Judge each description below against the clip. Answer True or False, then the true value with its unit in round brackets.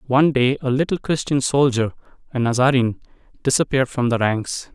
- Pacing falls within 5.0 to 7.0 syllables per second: True (5.9 syllables/s)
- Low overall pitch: True (130 Hz)